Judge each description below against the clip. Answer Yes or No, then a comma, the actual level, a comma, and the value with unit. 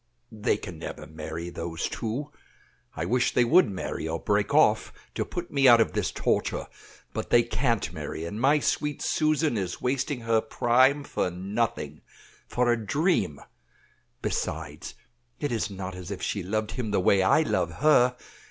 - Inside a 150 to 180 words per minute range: Yes, average, 170 wpm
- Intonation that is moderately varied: No, wide, 5.8 semitones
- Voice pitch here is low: Yes, low, 110 Hz